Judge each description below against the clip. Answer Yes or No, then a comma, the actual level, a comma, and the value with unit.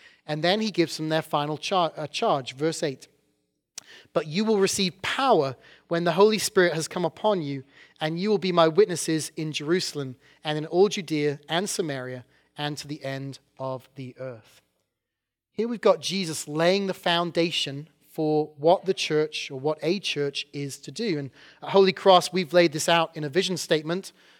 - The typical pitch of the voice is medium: Yes, medium, 155 Hz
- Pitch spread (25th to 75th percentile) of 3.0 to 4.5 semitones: Yes, average, 3.9 semitones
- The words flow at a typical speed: Yes, average, 185 wpm